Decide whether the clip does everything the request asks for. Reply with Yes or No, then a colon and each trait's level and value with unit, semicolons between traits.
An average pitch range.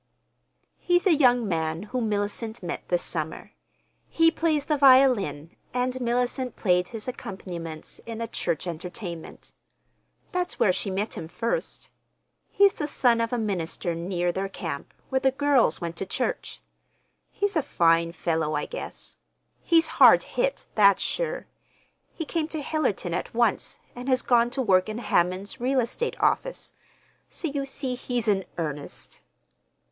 No: wide, 7.2 semitones